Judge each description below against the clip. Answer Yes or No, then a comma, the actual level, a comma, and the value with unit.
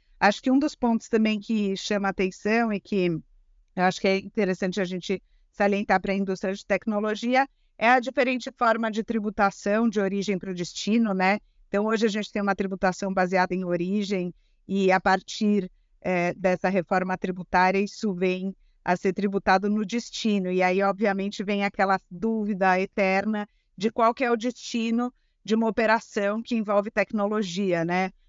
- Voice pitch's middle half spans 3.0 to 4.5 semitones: No, narrow, 2.6 semitones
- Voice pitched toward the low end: No, high, 200 Hz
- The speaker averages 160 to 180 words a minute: Yes, average, 170 wpm